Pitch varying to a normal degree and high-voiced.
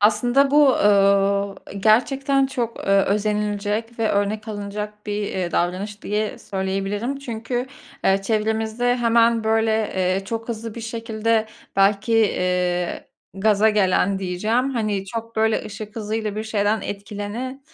No: narrow, 2.2 semitones; high, 215 Hz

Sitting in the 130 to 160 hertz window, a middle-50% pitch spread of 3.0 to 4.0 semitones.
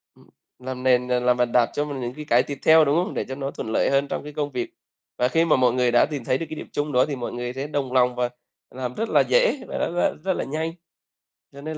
Yes: low, 135 Hz; average, 3.3 semitones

